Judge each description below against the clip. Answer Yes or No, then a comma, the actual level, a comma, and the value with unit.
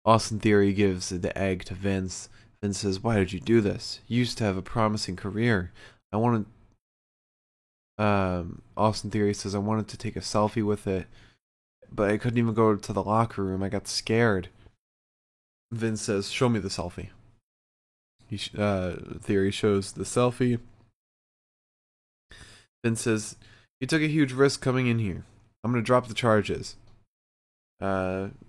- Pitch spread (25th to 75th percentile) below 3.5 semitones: Yes, average, 2.8 semitones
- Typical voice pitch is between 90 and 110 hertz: Yes, low, 105 Hz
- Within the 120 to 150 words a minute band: No, average, 160 wpm